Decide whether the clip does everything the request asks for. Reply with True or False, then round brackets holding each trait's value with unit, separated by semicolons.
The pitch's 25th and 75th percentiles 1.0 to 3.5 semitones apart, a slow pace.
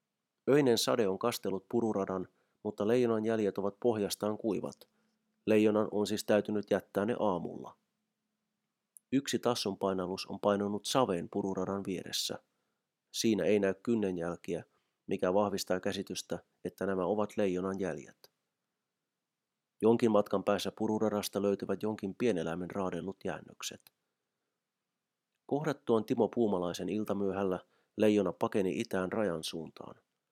False (2.9 semitones; 110 wpm)